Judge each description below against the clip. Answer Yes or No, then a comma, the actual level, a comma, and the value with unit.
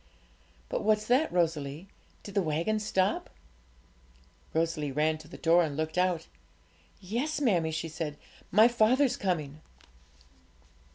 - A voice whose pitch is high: No, medium, 175 Hz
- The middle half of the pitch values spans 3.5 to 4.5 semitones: No, average, 5.3 semitones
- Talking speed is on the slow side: Yes, slow, 125 wpm